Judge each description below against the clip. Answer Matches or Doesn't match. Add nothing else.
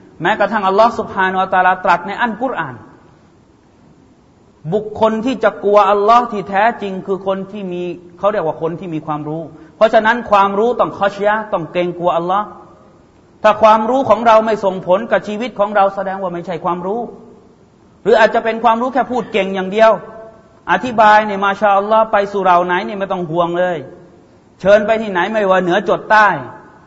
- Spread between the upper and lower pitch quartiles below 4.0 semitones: Matches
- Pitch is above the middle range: Matches